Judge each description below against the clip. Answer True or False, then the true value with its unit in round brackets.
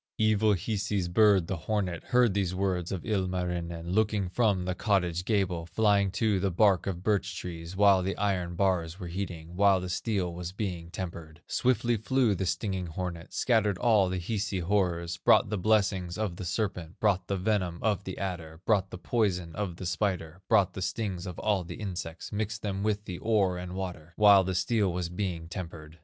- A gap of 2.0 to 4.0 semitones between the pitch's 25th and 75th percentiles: True (2.8 semitones)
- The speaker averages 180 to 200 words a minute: True (190 wpm)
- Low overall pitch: True (95 Hz)